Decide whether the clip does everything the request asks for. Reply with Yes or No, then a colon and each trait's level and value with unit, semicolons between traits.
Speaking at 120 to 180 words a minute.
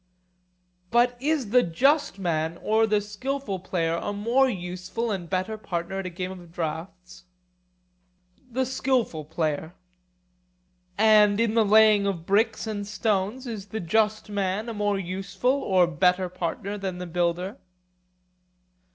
Yes: average, 140 wpm